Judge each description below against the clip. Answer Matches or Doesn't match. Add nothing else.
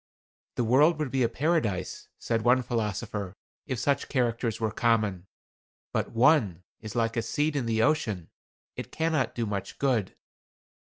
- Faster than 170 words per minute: Doesn't match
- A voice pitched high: Doesn't match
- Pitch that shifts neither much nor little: Matches